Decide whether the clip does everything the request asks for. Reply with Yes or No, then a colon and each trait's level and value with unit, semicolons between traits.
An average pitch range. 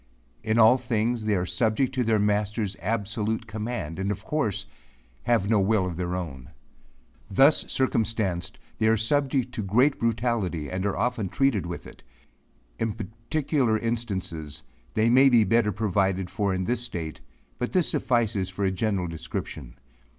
Yes: average, 3.8 semitones